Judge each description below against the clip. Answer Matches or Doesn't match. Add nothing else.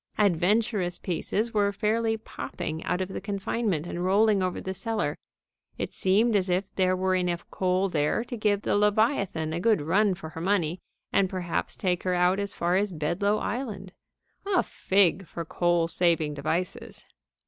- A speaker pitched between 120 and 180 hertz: Doesn't match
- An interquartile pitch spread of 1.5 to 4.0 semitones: Matches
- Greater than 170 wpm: Doesn't match